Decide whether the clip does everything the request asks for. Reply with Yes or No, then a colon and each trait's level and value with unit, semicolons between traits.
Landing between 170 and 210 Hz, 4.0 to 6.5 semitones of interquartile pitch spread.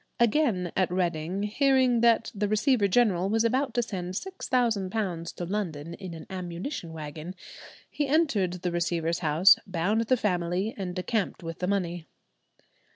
Yes: high, 190 Hz; average, 4.7 semitones